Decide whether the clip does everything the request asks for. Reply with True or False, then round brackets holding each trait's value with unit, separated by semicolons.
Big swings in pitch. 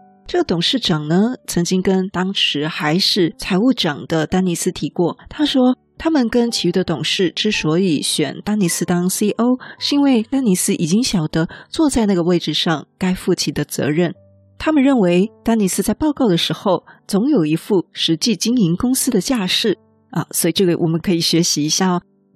False (4.7 semitones)